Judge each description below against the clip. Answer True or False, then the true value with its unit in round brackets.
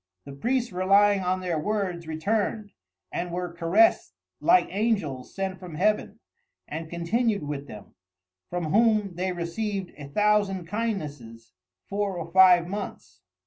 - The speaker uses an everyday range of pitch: True (3.8 semitones)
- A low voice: False (185 Hz)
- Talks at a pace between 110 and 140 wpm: True (135 wpm)